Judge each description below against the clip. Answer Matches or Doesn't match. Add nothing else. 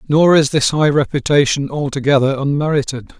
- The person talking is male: Matches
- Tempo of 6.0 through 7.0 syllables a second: Doesn't match